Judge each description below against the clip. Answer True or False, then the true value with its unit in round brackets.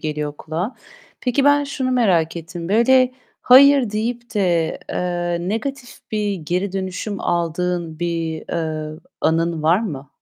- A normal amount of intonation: False (6.0 semitones)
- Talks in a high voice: False (180 Hz)